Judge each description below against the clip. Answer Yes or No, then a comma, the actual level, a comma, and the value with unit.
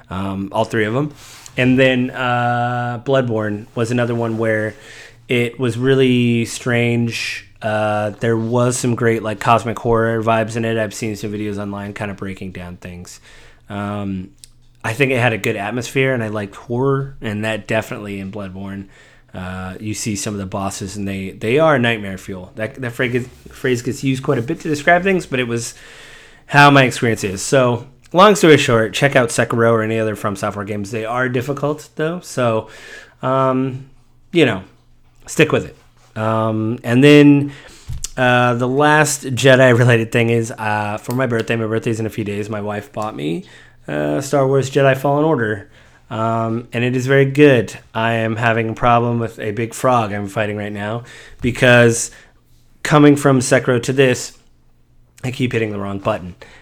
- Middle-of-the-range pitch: No, low, 115 Hz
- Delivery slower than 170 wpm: No, average, 180 wpm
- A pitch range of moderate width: Yes, average, 3.3 semitones